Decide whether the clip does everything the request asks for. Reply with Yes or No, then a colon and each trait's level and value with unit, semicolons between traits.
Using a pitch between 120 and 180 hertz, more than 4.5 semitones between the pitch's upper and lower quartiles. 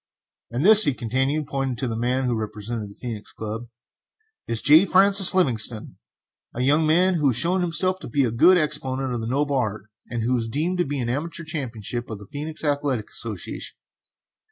Yes: low, 135 Hz; average, 5.1 semitones